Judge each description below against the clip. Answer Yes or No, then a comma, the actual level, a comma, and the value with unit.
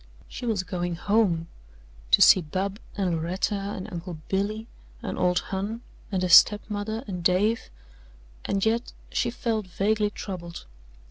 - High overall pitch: Yes, high, 195 Hz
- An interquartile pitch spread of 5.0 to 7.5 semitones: No, average, 3.0 semitones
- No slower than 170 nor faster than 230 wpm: No, average, 145 wpm